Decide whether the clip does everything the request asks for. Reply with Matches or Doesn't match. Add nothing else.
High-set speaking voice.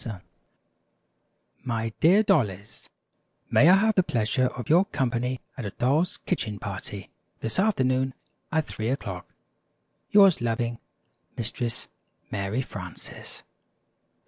Doesn't match